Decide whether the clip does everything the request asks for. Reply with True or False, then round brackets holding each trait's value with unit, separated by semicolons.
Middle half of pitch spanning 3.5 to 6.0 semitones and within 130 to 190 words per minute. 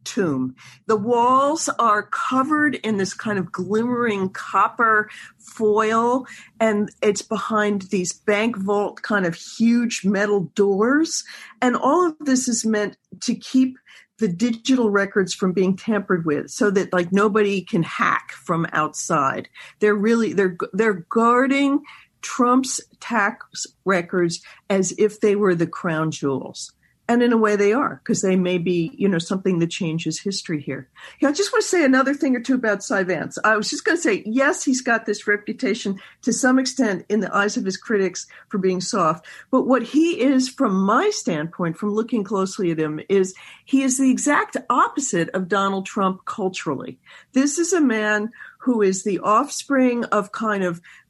True (4.6 semitones; 170 wpm)